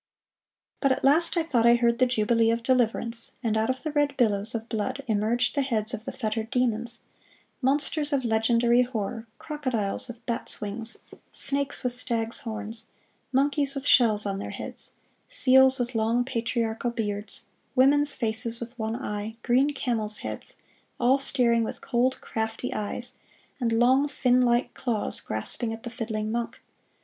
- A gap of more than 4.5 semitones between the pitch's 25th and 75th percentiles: No, narrow, 2.6 semitones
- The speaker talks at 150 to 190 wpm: Yes, average, 160 wpm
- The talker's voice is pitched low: No, high, 235 Hz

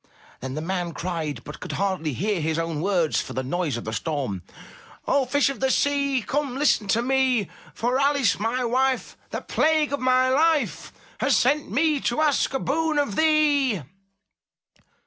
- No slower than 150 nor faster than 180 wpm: Yes, average, 175 wpm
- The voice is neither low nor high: No, very high, 250 Hz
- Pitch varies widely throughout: Yes, wide, 8.7 semitones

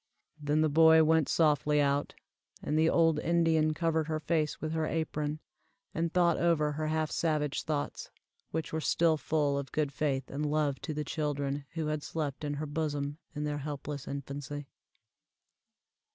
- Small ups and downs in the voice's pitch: Yes, narrow, 1.6 semitones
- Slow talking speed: No, average, 165 wpm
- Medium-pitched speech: Yes, medium, 150 Hz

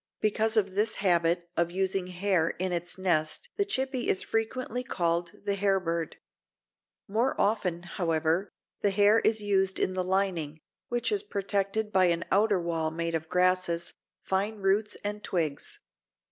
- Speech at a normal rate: Yes, average, 150 wpm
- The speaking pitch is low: No, high, 190 Hz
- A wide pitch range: No, average, 3.4 semitones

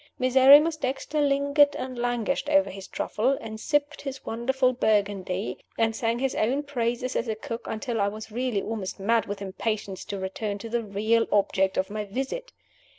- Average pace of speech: Yes, average, 175 wpm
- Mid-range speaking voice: No, high, 230 Hz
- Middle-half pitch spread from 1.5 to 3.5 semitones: No, average, 4.3 semitones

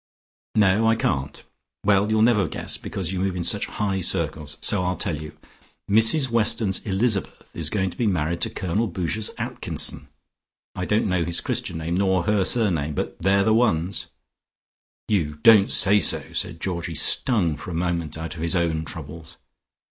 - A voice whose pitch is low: Yes, very low, 95 Hz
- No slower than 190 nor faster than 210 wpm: No, average, 175 wpm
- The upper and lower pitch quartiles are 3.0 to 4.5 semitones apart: Yes, average, 4.0 semitones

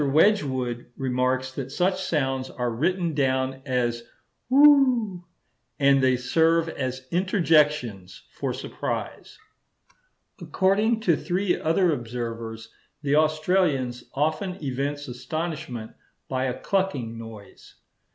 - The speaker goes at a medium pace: No, slow, 100 wpm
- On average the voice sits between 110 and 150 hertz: Yes, medium, 140 Hz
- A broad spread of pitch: Yes, wide, 5.7 semitones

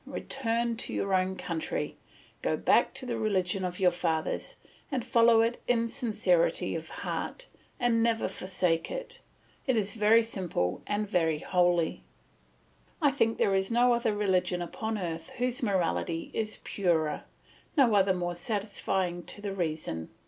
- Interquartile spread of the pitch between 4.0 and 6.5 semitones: Yes, average, 4.7 semitones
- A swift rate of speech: No, average, 150 wpm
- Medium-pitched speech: No, high, 205 Hz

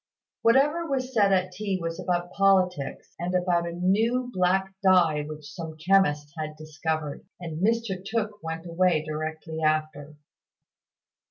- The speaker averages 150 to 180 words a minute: No, average, 140 wpm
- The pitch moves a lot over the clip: No, average, 3.8 semitones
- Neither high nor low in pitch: Yes, medium, 180 Hz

